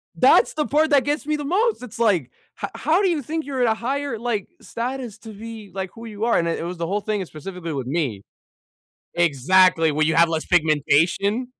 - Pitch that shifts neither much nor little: No, wide, 7.5 semitones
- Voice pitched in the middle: No, high, 210 Hz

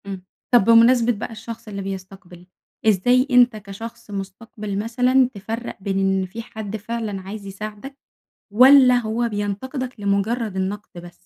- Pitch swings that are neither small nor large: Yes, average, 3.3 semitones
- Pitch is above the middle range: Yes, high, 215 Hz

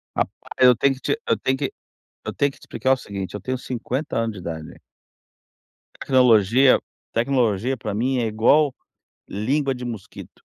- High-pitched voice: No, low, 125 Hz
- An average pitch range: Yes, average, 3.5 semitones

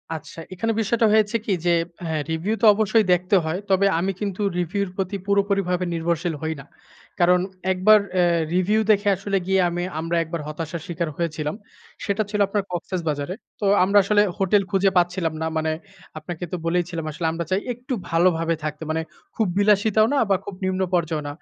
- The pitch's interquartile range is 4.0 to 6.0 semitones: No, average, 3.3 semitones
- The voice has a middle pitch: Yes, medium, 180 Hz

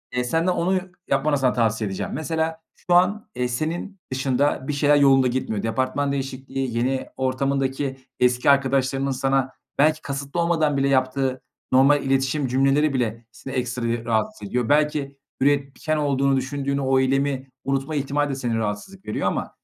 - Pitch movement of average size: No, narrow, 1.9 semitones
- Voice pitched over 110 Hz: Yes, low, 135 Hz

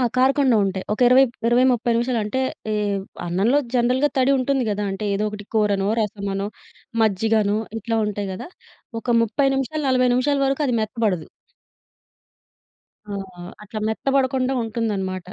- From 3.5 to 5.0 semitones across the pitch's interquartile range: Yes, average, 4.1 semitones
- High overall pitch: Yes, high, 230 Hz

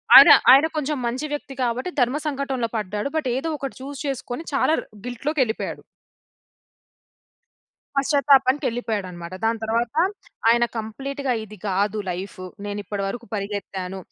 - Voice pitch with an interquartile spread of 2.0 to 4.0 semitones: No, average, 5.0 semitones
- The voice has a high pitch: Yes, high, 240 Hz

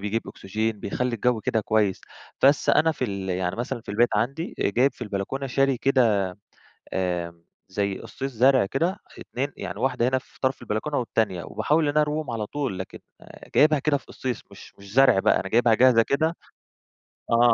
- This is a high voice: No, low, 120 Hz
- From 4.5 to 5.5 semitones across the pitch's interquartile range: Yes, average, 5.0 semitones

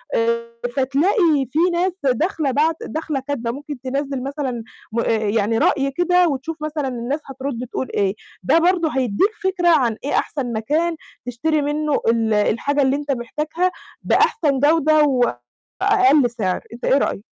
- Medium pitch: No, very high, 280 Hz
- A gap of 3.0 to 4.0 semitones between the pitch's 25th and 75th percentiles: No, average, 4.6 semitones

